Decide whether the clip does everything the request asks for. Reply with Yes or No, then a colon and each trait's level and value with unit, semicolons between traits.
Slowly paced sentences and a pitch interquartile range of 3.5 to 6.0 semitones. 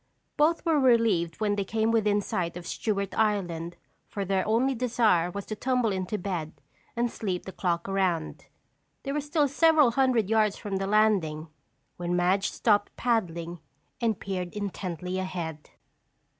No: average, 155 wpm; average, 4.3 semitones